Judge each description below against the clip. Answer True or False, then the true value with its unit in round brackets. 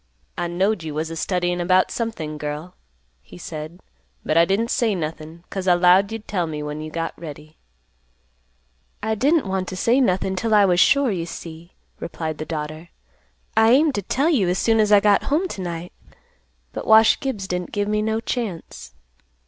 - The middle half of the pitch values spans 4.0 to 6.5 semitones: True (4.9 semitones)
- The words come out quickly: False (190 wpm)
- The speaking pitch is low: False (185 Hz)